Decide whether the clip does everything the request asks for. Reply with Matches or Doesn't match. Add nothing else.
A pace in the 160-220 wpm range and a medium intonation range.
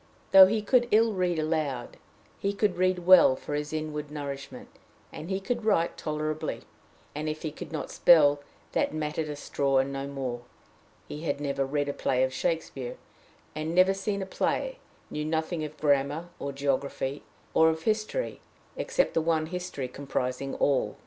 Matches